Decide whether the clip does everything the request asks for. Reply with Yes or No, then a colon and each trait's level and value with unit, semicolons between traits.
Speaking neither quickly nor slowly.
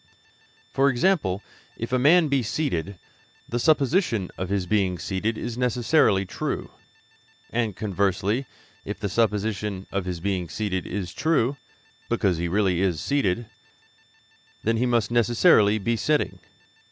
No: slow, 130 wpm